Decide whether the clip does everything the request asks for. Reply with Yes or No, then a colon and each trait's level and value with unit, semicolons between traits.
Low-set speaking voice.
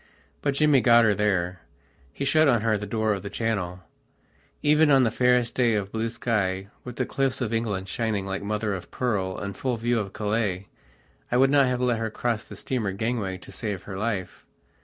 Yes: low, 110 Hz